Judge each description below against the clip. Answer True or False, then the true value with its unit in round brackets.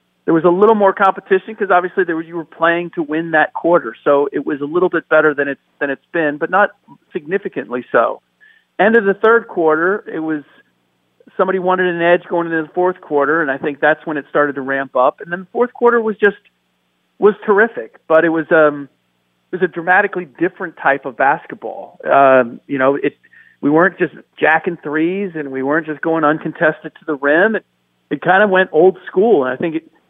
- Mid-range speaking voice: True (165 Hz)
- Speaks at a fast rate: True (215 wpm)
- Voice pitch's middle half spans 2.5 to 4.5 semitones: True (4.1 semitones)